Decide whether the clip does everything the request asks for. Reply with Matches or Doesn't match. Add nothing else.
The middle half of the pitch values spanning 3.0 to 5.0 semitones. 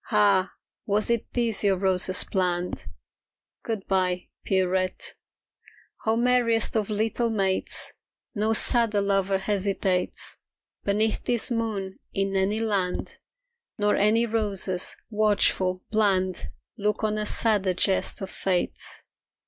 Doesn't match